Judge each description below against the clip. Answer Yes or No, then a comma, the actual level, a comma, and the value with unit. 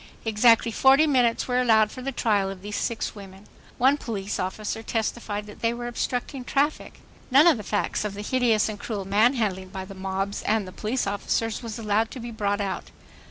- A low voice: No, high, 220 Hz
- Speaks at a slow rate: No, average, 195 wpm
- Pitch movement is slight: No, average, 3.1 semitones